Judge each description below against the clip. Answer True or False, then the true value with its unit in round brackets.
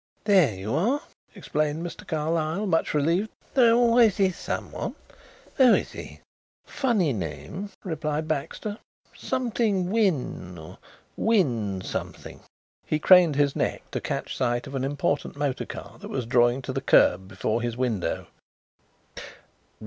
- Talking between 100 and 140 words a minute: True (135 wpm)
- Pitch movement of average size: False (8.4 semitones)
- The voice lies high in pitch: False (155 Hz)